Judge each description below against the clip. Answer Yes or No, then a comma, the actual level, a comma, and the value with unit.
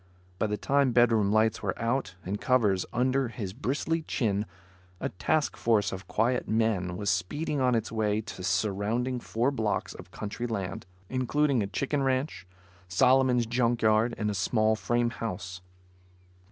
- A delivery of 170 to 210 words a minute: No, average, 155 wpm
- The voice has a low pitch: Yes, low, 115 Hz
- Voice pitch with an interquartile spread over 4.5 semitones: No, average, 3.7 semitones